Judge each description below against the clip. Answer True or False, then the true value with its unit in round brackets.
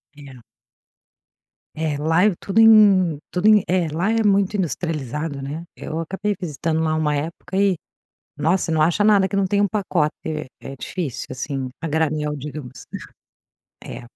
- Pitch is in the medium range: True (165 Hz)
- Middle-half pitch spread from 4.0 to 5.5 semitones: True (4.5 semitones)